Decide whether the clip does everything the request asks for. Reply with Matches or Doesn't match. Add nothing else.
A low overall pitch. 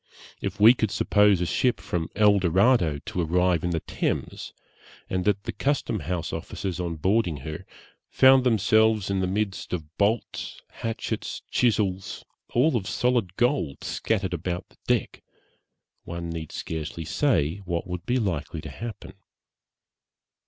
Matches